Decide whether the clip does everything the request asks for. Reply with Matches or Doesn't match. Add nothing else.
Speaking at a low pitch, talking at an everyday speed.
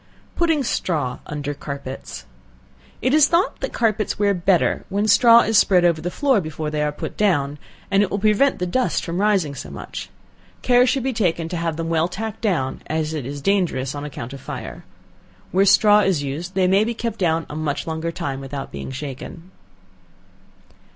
Doesn't match